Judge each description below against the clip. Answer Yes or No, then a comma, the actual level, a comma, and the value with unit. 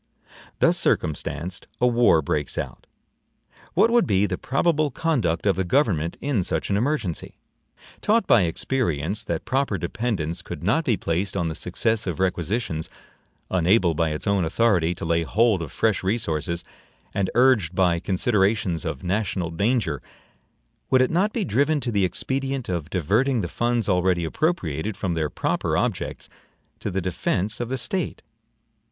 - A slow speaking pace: No, average, 160 wpm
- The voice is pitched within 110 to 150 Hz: No, low, 100 Hz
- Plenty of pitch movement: Yes, wide, 6.2 semitones